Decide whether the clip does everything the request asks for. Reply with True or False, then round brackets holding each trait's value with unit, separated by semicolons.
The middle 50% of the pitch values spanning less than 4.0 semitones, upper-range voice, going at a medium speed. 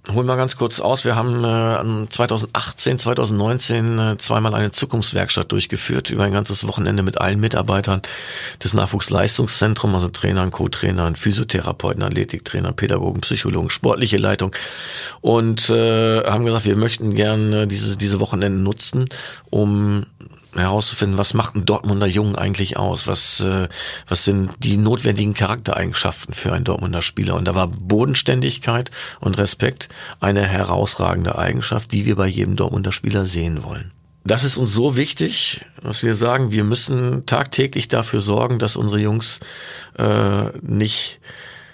False (2.9 semitones; 105 Hz; 140 wpm)